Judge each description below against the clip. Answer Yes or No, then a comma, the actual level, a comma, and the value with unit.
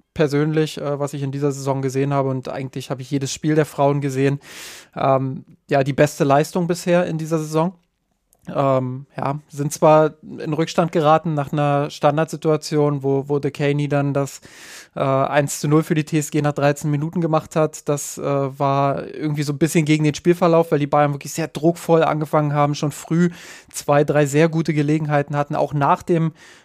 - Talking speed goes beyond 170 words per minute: Yes, average, 185 wpm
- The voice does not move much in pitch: Yes, narrow, 2.1 semitones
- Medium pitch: Yes, medium, 150 Hz